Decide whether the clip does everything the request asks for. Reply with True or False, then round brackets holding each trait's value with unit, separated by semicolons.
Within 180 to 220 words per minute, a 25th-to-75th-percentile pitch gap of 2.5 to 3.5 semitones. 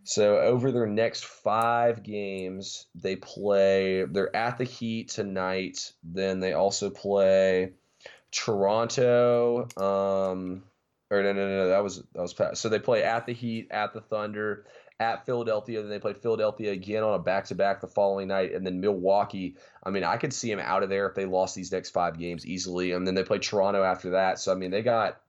True (195 wpm; 2.8 semitones)